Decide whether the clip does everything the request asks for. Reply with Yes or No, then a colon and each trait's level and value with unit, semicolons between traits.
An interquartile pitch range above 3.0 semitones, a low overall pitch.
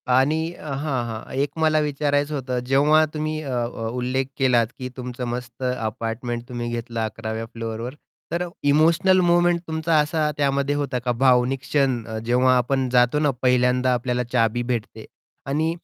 Yes: average, 3.4 semitones; low, 130 Hz